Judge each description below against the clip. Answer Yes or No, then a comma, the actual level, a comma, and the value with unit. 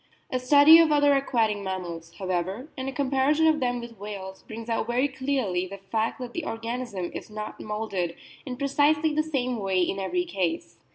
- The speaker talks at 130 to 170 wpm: No, average, 185 wpm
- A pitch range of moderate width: No, wide, 6.2 semitones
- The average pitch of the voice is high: Yes, high, 235 Hz